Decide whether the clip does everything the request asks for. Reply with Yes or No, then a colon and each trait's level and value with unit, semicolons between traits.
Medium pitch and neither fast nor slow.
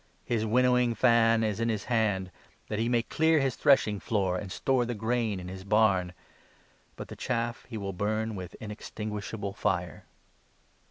No: low, 110 Hz; average, 170 wpm